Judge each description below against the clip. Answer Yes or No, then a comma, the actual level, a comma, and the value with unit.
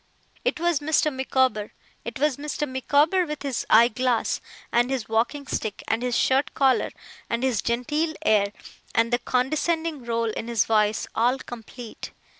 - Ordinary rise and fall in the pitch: Yes, average, 4.0 semitones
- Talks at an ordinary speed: Yes, average, 160 wpm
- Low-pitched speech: No, very high, 250 Hz